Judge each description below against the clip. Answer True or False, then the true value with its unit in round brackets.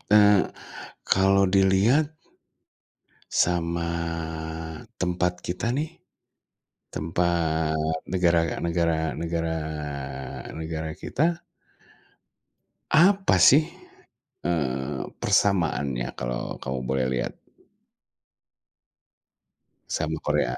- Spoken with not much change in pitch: False (3.7 semitones)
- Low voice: True (85 Hz)